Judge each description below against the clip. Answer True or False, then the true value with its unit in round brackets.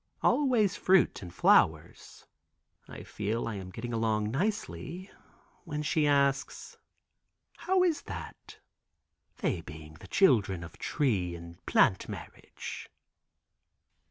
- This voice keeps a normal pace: False (110 wpm)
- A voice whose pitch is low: True (115 Hz)